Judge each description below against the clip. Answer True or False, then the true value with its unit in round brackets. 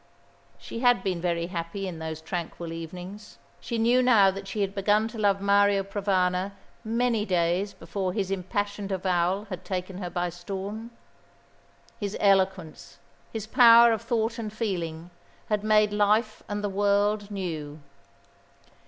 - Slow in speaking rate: False (145 wpm)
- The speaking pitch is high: True (195 Hz)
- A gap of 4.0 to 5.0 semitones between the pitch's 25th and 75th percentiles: False (2.8 semitones)